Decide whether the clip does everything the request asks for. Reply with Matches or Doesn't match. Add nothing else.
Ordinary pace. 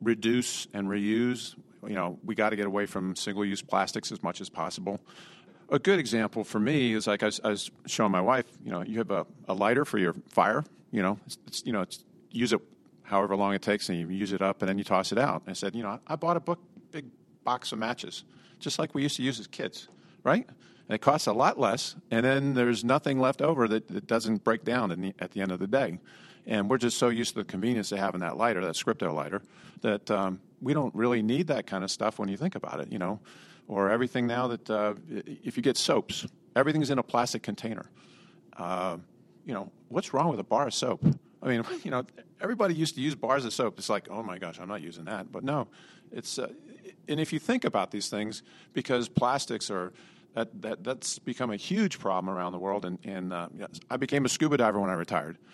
Doesn't match